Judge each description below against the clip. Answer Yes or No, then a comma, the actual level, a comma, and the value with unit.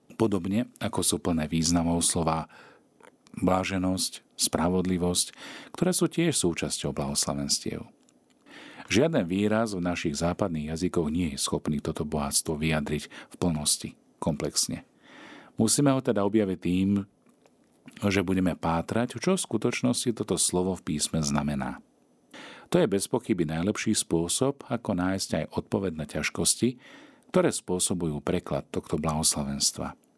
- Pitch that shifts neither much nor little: Yes, average, 4.7 semitones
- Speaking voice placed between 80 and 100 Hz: Yes, very low, 90 Hz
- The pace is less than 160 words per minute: Yes, average, 120 wpm